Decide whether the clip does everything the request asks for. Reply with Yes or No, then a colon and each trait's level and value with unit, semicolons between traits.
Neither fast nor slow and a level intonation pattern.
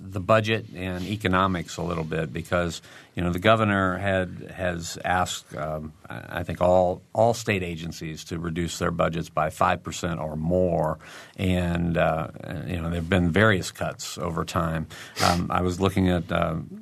Yes: average, 170 wpm; narrow, 2.0 semitones